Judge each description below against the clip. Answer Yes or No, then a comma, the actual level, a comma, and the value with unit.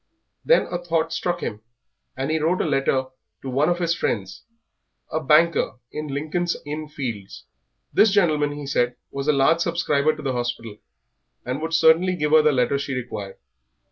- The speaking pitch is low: No, medium, 150 Hz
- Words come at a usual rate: Yes, average, 175 wpm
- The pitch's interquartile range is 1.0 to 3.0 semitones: No, average, 3.7 semitones